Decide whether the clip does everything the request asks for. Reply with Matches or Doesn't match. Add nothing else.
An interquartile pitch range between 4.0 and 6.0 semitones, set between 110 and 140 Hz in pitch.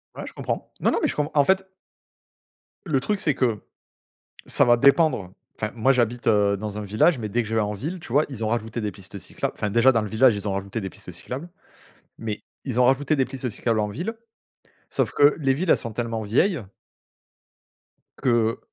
Matches